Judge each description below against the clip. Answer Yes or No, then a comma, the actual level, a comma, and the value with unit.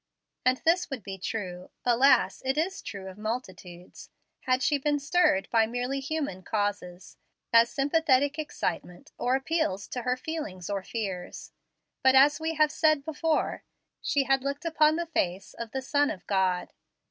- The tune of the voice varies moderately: No, wide, 7.0 semitones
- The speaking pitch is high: Yes, very high, 260 Hz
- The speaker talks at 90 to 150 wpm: No, average, 160 wpm